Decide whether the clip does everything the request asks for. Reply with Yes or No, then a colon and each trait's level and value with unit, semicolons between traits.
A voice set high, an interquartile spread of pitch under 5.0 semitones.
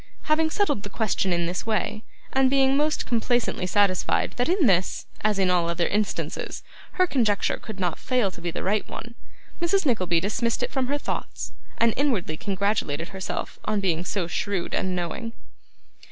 No: high, 210 Hz; wide, 5.6 semitones